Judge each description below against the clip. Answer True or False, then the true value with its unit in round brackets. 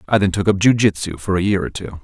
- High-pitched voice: False (95 Hz)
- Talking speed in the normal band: False (325 wpm)